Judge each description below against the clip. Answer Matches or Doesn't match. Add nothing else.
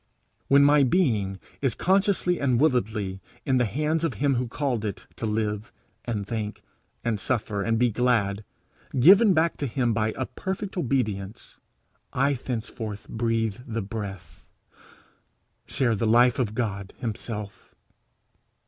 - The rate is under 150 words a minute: Matches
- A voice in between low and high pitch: Doesn't match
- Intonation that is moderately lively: Matches